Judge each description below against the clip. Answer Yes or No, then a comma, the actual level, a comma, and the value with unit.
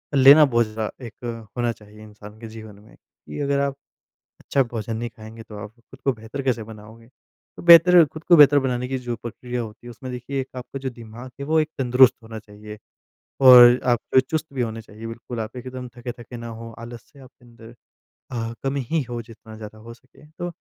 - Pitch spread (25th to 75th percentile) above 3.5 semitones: No, average, 2.9 semitones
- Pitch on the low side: Yes, low, 120 Hz